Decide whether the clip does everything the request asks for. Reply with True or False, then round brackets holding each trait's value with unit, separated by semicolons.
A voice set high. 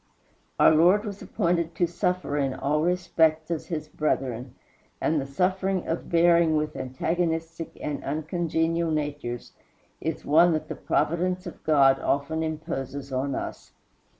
False (160 Hz)